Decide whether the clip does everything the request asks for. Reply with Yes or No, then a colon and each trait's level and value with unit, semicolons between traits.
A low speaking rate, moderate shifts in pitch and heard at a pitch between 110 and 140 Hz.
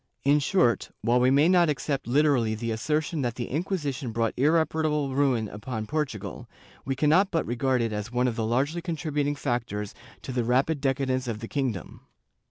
No: average, 180 wpm; average, 4.2 semitones; low, 135 Hz